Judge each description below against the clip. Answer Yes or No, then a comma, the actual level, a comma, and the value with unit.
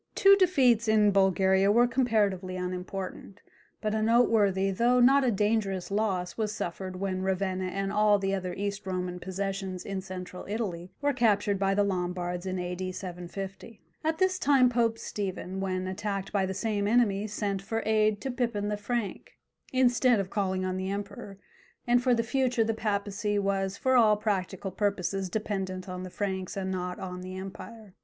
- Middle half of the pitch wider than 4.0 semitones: No, average, 2.8 semitones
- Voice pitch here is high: Yes, high, 200 Hz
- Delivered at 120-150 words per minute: No, average, 175 wpm